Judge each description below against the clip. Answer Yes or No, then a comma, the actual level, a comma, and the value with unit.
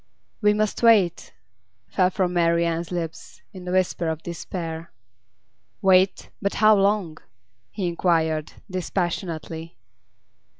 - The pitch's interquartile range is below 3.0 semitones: Yes, narrow, 2.6 semitones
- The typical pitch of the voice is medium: Yes, medium, 175 Hz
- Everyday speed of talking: No, slow, 110 wpm